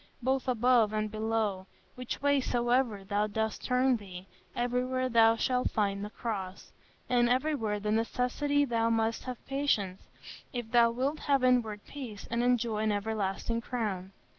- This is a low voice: No, high, 230 Hz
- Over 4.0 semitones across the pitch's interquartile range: No, average, 3.0 semitones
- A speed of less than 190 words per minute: Yes, average, 150 wpm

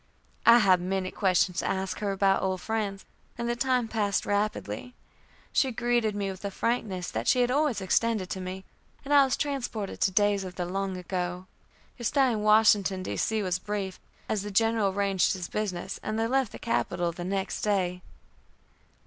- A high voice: Yes, high, 200 Hz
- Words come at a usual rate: Yes, average, 185 wpm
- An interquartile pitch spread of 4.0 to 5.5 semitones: No, average, 3.3 semitones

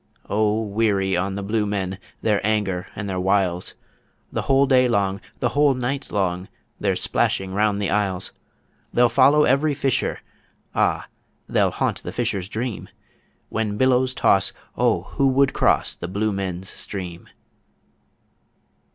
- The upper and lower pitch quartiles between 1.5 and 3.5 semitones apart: No, average, 4.6 semitones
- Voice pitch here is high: No, low, 105 Hz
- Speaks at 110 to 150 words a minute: Yes, average, 145 wpm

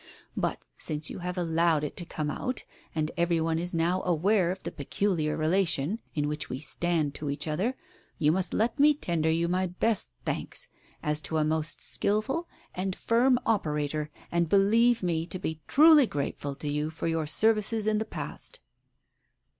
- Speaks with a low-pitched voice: No, medium, 170 Hz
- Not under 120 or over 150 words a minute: No, average, 180 wpm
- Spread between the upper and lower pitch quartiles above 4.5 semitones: Yes, average, 4.9 semitones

